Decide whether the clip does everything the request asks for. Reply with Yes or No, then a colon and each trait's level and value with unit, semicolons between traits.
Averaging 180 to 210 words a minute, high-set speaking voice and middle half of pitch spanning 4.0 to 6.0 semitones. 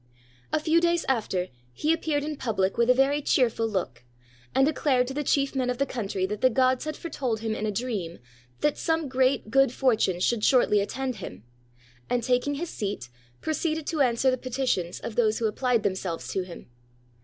Yes: average, 200 wpm; very high, 250 Hz; average, 4.7 semitones